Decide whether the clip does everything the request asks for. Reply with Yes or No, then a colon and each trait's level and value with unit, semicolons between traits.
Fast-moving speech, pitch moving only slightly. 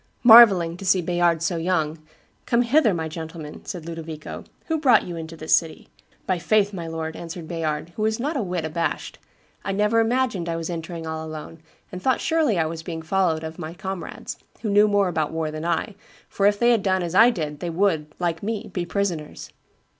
No: fast, 210 wpm; average, 3.9 semitones